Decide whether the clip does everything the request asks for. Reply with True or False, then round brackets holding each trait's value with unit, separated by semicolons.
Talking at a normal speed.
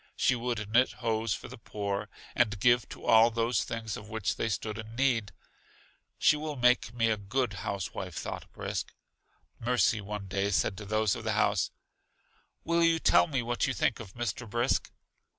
True (185 wpm)